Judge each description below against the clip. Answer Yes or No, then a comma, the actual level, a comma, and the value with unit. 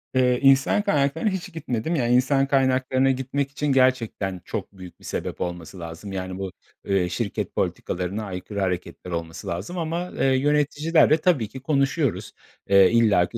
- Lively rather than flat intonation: Yes, wide, 6.6 semitones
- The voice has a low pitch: Yes, low, 130 Hz